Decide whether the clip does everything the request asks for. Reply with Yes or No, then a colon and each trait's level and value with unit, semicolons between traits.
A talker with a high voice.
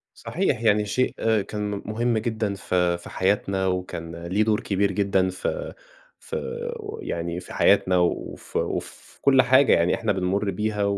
No: low, 100 Hz